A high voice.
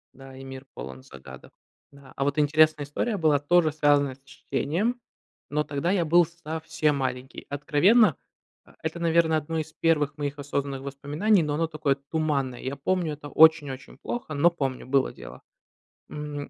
No: medium, 145 Hz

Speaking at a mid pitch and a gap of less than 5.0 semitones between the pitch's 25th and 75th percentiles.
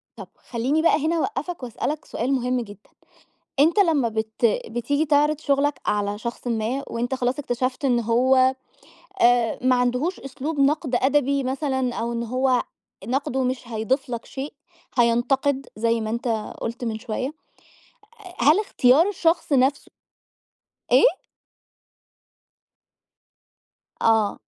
No: very high, 255 Hz; average, 3.3 semitones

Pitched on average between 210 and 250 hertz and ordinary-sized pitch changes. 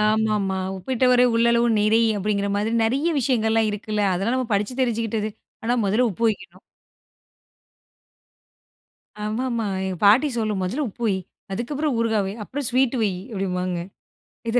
Yes: high, 220 Hz; average, 3.1 semitones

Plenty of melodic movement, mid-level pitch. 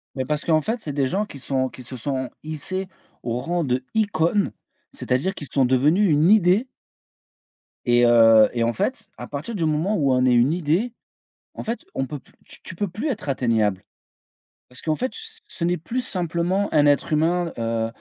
Yes: wide, 6.6 semitones; medium, 155 Hz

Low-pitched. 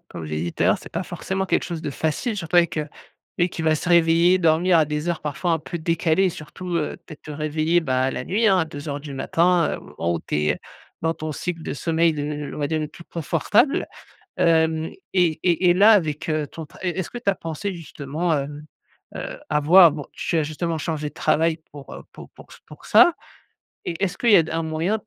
No: medium, 160 Hz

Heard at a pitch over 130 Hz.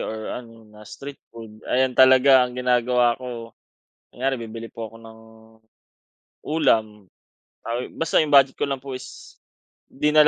No: low, 125 Hz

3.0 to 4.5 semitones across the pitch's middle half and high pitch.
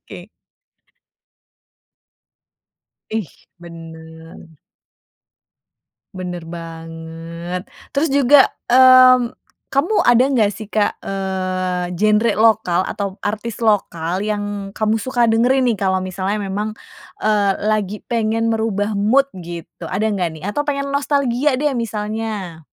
Yes: average, 4.1 semitones; high, 210 Hz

